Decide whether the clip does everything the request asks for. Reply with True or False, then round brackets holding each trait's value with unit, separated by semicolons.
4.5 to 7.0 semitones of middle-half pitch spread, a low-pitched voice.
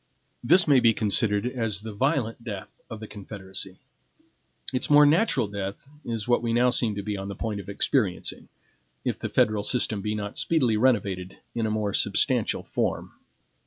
False (3.3 semitones; 110 Hz)